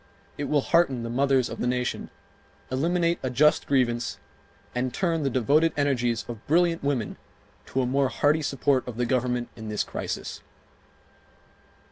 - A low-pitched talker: Yes, low, 130 Hz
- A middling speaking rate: Yes, average, 155 wpm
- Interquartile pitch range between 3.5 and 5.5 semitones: No, average, 3.1 semitones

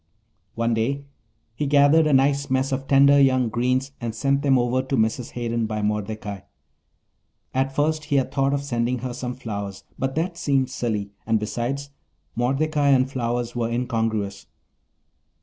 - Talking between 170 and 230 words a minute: No, average, 160 wpm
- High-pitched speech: No, low, 130 Hz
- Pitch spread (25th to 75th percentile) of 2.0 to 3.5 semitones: Yes, average, 3.1 semitones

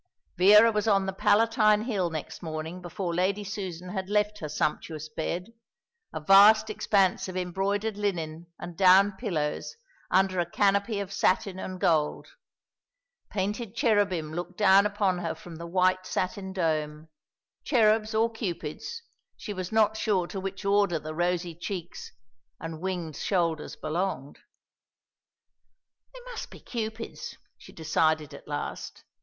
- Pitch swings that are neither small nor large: Yes, average, 3.5 semitones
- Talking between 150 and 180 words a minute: No, average, 140 wpm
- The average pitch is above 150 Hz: Yes, high, 190 Hz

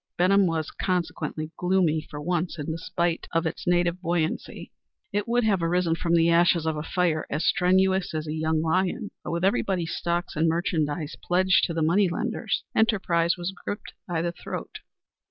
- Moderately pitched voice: Yes, medium, 170 Hz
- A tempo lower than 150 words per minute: No, average, 175 wpm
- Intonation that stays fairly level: Yes, narrow, 2.3 semitones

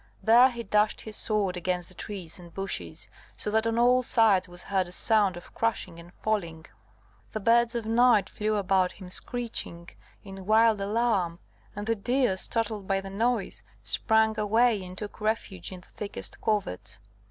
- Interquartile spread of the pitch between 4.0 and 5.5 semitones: No, average, 3.5 semitones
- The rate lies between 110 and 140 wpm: No, average, 175 wpm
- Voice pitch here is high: Yes, high, 210 Hz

